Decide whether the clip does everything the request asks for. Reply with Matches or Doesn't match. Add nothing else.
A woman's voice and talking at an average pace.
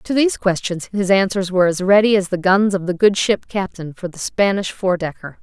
Doesn't match